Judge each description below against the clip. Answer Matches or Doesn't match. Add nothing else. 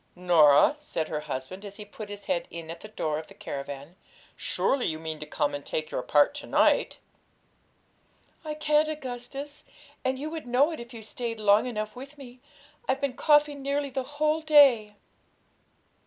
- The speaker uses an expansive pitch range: Matches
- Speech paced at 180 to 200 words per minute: Matches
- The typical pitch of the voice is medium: Doesn't match